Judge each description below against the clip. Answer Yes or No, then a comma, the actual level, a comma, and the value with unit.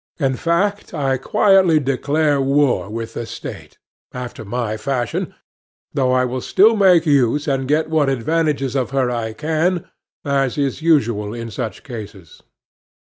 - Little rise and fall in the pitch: No, average, 4.3 semitones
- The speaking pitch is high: No, low, 135 Hz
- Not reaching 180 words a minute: Yes, average, 145 wpm